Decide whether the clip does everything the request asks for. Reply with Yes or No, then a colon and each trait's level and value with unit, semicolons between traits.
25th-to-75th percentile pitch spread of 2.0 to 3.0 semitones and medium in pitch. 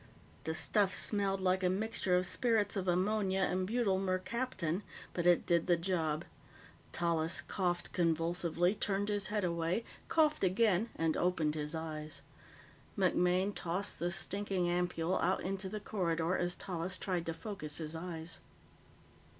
Yes: narrow, 2.6 semitones; medium, 180 Hz